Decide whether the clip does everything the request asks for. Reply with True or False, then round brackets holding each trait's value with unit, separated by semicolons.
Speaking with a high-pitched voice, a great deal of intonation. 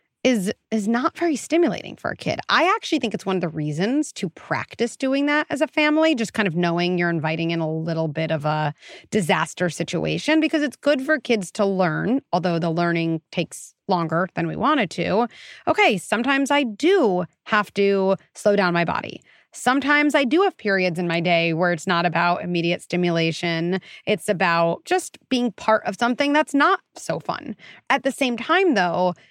True (200 Hz; 8.3 semitones)